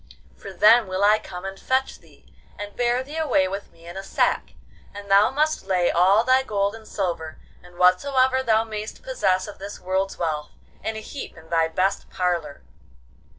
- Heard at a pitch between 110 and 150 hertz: No, high, 200 Hz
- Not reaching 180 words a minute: No, average, 190 wpm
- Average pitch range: Yes, average, 4.0 semitones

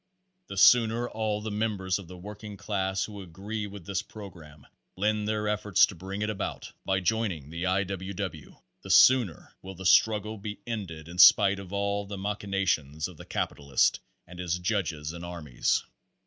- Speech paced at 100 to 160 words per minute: No, average, 175 wpm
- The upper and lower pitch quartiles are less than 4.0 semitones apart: Yes, average, 3.0 semitones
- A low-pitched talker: Yes, low, 100 Hz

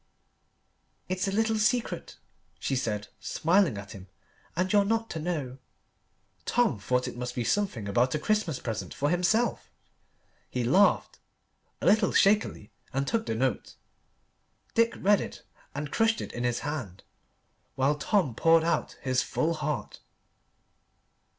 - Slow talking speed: No, average, 145 wpm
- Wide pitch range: Yes, wide, 8.4 semitones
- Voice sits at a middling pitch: Yes, medium, 155 Hz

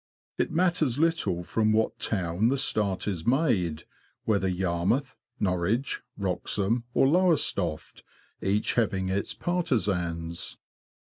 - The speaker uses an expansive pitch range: Yes, wide, 6.7 semitones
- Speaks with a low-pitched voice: Yes, low, 105 Hz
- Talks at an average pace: No, slow, 110 wpm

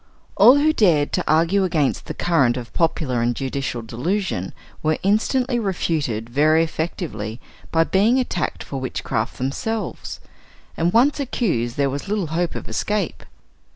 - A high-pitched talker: No, medium, 160 Hz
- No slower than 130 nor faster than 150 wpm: Yes, average, 145 wpm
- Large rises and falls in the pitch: Yes, wide, 7.4 semitones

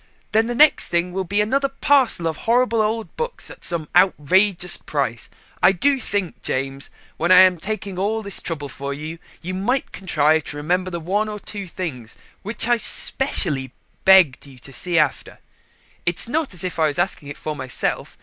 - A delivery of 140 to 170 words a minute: No, average, 190 wpm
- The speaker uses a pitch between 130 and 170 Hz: No, medium, 185 Hz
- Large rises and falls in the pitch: Yes, wide, 5.7 semitones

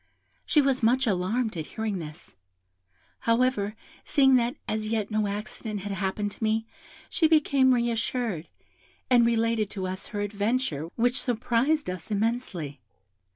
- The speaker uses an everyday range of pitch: Yes, average, 3.6 semitones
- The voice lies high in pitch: Yes, high, 220 Hz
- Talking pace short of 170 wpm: Yes, average, 145 wpm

